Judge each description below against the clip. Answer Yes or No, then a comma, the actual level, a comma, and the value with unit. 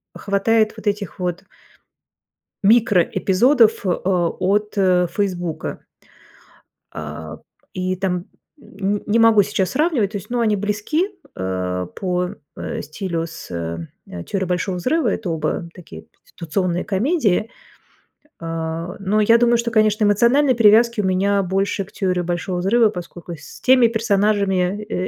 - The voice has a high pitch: Yes, high, 195 Hz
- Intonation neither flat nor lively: Yes, average, 3.4 semitones